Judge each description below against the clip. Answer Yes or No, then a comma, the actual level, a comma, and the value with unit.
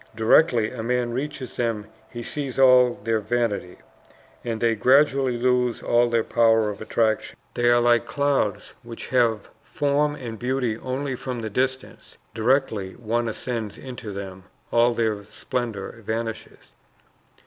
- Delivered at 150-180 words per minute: No, average, 140 wpm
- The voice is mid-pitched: No, low, 120 Hz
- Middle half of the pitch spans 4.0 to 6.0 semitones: No, narrow, 2.4 semitones